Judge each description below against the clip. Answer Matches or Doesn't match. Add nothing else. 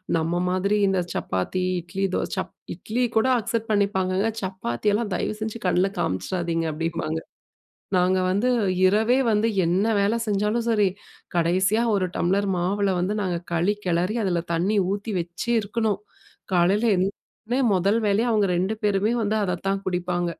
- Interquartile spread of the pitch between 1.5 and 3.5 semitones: Matches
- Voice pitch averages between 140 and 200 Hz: Matches